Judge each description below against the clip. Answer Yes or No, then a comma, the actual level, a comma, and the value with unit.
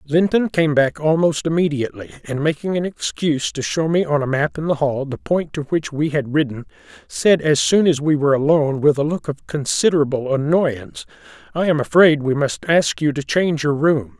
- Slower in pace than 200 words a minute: No, fast, 205 wpm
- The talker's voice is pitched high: No, medium, 150 Hz